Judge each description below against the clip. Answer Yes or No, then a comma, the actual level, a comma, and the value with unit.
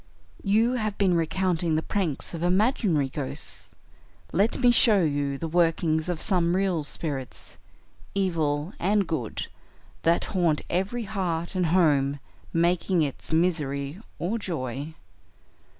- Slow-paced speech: Yes, slow, 125 wpm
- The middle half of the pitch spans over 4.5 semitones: No, average, 3.8 semitones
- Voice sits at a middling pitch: Yes, medium, 170 Hz